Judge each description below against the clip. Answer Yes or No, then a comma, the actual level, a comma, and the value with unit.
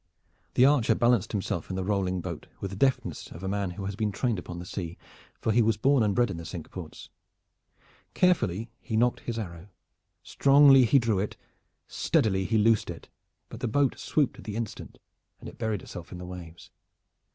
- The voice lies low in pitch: Yes, low, 105 Hz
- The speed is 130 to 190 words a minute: No, average, 200 wpm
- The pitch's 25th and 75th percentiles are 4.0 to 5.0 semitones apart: Yes, average, 4.3 semitones